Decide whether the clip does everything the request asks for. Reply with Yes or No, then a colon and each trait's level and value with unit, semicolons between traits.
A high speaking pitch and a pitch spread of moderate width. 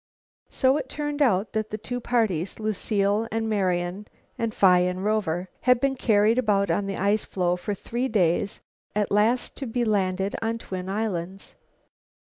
Yes: high, 210 Hz; average, 3.3 semitones